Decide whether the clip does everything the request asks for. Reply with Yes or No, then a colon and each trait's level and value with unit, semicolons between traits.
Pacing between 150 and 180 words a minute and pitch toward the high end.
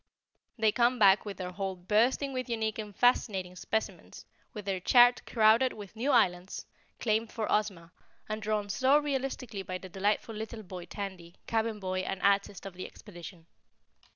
Yes: average, 165 wpm; high, 210 Hz